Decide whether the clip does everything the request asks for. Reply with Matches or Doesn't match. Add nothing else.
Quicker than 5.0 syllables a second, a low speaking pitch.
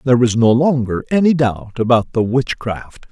Doesn't match